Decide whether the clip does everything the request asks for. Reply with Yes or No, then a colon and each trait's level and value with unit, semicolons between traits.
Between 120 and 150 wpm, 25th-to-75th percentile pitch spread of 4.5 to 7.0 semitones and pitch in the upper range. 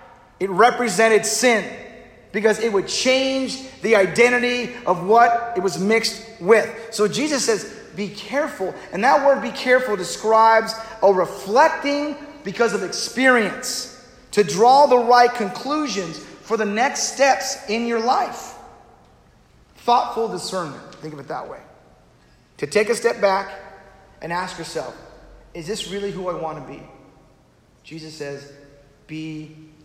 Yes: average, 140 wpm; average, 5.1 semitones; high, 220 Hz